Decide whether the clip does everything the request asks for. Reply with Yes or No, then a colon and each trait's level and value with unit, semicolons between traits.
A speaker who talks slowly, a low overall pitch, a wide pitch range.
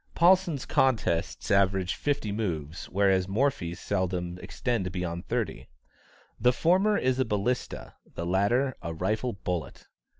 Yes: slow, 125 wpm; low, 100 Hz; wide, 6.0 semitones